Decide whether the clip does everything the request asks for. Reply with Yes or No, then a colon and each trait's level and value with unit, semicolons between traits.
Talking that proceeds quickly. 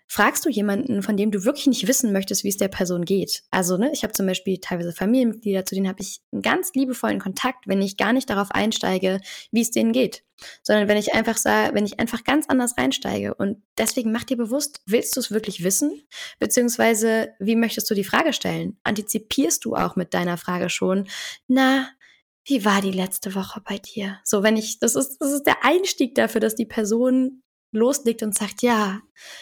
Yes: fast, 210 wpm